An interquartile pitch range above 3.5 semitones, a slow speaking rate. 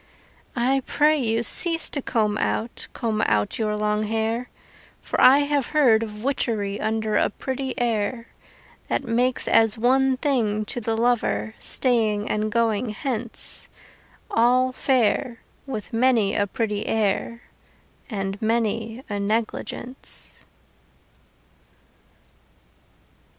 No: average, 3.0 semitones; slow, 115 wpm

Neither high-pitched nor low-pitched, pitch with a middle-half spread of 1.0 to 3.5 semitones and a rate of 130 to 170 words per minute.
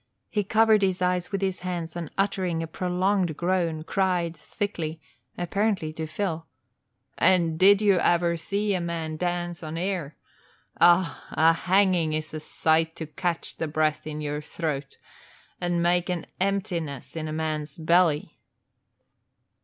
Yes: medium, 170 Hz; average, 2.8 semitones; average, 145 wpm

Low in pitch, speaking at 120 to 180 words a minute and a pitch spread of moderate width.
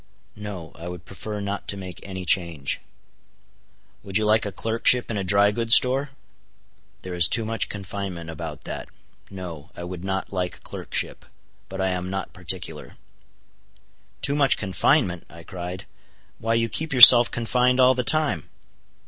Yes: low, 100 Hz; average, 160 wpm; average, 4.1 semitones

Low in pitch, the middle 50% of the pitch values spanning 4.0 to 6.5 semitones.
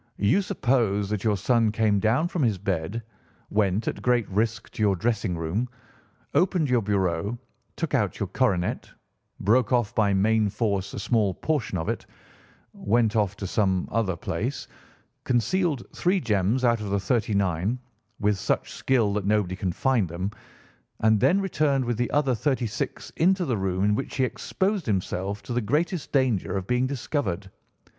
Yes: low, 110 Hz; average, 4.4 semitones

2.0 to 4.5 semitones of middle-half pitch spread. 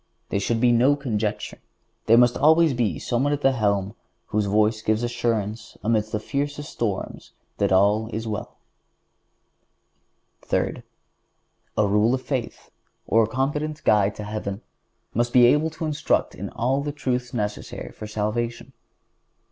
Yes: average, 3.8 semitones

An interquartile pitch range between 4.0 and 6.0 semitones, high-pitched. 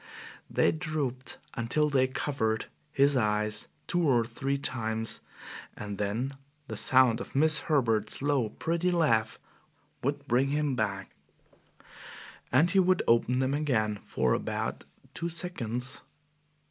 No: average, 5.1 semitones; low, 130 Hz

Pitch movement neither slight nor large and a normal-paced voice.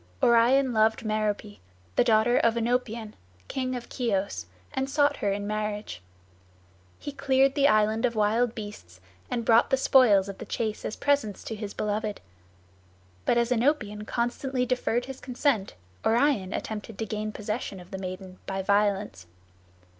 Yes: average, 3.2 semitones; average, 155 wpm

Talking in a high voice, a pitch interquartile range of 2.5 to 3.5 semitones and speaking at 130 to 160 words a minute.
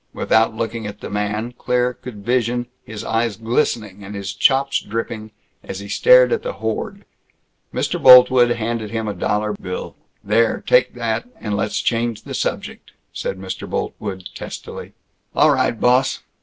No: low, 115 Hz; average, 2.9 semitones; average, 155 wpm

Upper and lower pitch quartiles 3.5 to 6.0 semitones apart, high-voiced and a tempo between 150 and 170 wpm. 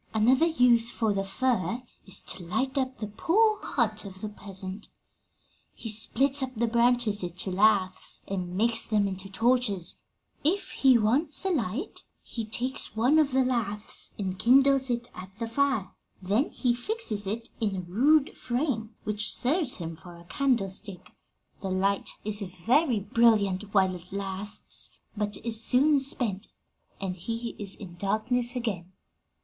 Yes: average, 4.5 semitones; high, 220 Hz; average, 155 wpm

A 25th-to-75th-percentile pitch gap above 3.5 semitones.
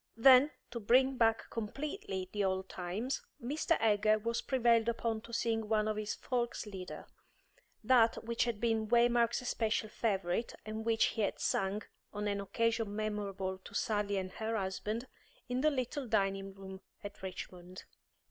No: average, 2.8 semitones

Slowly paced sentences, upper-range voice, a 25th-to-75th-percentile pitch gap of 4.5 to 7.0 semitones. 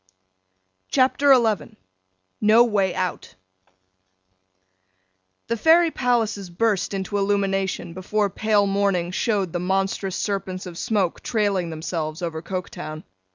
No: slow, 110 wpm; high, 195 Hz; average, 2.9 semitones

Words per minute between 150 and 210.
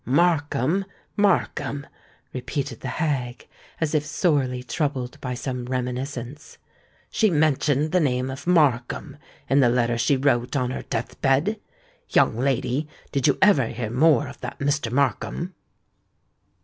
No: slow, 135 wpm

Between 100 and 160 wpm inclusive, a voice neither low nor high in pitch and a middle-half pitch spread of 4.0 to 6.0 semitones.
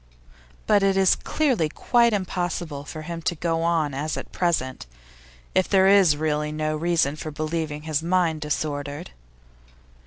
No: average, 150 wpm; medium, 160 Hz; average, 3.0 semitones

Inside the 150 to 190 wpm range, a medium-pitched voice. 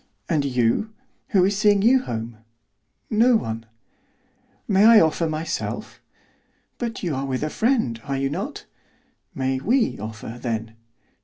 No: average, 140 wpm; medium, 155 Hz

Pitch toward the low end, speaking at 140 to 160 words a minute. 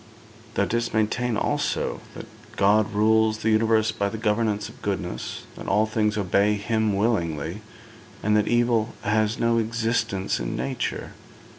Yes: low, 110 Hz; average, 145 wpm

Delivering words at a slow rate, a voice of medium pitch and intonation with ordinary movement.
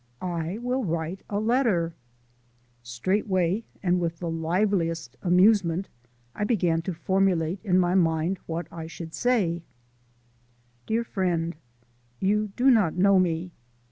Yes: slow, 125 wpm; medium, 180 Hz; average, 3.5 semitones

